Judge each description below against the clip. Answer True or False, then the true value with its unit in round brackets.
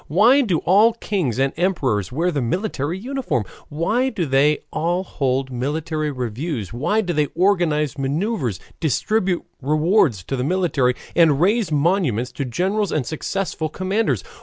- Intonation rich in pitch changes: True (6.0 semitones)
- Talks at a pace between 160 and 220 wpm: False (145 wpm)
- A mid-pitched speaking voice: True (155 Hz)